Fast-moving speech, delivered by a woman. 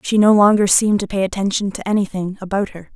Yes: fast, 225 wpm; female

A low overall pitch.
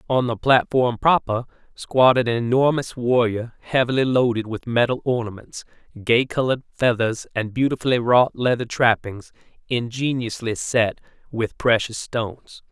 Yes: low, 120 Hz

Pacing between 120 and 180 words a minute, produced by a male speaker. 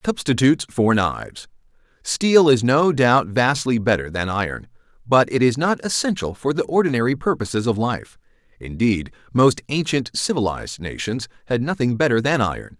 Yes: average, 145 wpm; male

